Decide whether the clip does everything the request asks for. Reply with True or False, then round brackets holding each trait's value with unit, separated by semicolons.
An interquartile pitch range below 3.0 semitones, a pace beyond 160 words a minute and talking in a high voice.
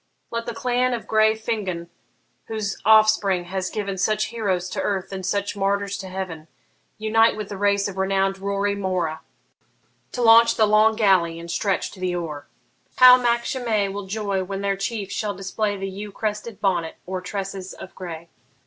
True (2.4 semitones; 175 wpm; 200 Hz)